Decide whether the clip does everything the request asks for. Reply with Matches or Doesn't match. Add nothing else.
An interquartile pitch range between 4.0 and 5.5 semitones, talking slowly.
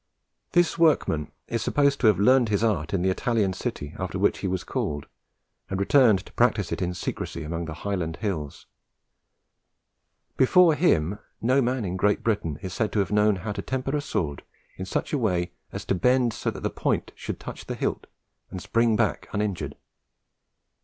Doesn't match